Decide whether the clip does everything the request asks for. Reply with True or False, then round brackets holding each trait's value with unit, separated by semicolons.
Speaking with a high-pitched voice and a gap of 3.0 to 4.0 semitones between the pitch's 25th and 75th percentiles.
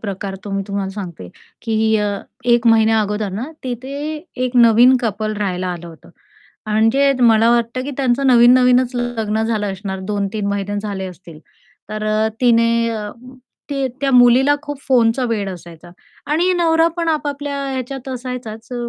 True (230 Hz; 3.7 semitones)